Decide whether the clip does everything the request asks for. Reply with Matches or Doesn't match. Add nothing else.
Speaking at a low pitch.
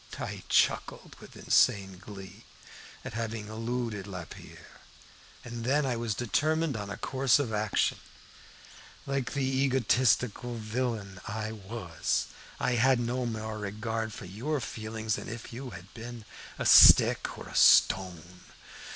Matches